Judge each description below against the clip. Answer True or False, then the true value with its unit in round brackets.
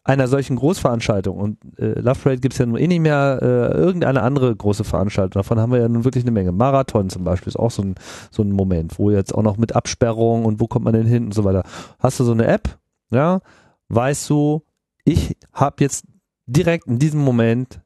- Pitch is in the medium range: False (115 Hz)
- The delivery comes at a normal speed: False (225 wpm)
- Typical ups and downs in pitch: True (4.2 semitones)